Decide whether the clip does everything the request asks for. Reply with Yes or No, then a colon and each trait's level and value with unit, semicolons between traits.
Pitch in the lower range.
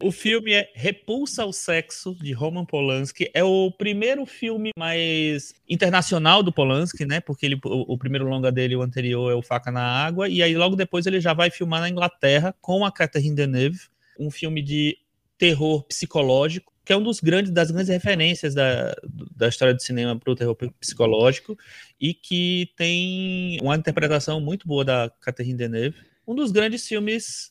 No: medium, 165 Hz